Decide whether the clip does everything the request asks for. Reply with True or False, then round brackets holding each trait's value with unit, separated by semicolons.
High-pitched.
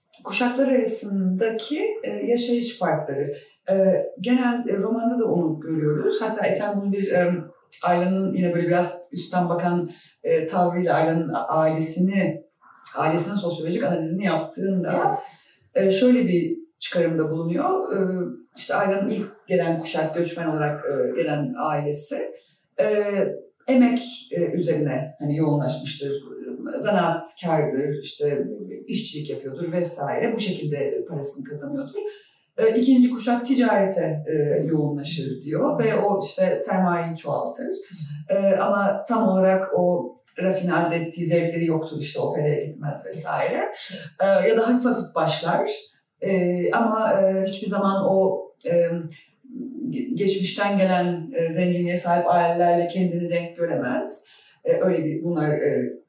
False (180 Hz)